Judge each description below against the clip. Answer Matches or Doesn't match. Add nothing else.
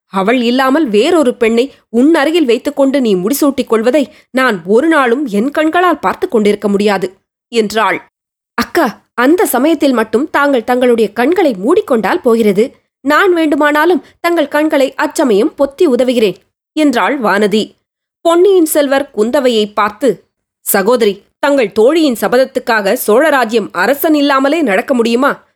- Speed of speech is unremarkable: Matches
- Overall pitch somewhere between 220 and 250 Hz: Doesn't match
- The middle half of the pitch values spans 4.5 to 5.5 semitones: Matches